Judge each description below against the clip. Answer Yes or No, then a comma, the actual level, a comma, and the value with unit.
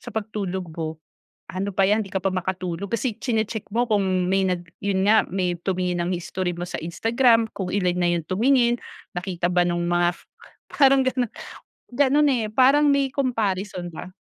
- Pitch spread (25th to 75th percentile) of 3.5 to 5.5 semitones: Yes, average, 4.8 semitones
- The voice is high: Yes, high, 195 Hz